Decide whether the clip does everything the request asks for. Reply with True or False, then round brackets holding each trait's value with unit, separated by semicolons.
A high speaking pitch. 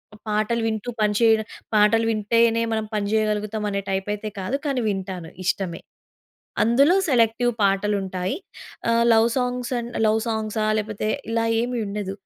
True (215 Hz)